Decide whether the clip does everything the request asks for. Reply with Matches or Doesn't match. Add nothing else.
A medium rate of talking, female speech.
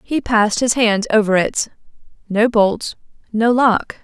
Matches